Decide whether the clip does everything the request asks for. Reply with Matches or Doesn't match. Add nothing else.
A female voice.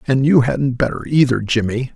Doesn't match